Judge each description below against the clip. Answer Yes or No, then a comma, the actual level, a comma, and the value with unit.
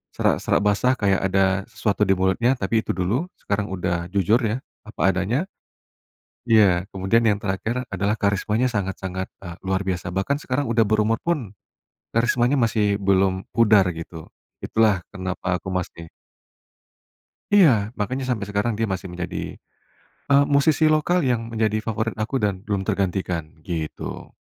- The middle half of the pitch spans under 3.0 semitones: No, average, 3.3 semitones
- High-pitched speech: No, low, 100 Hz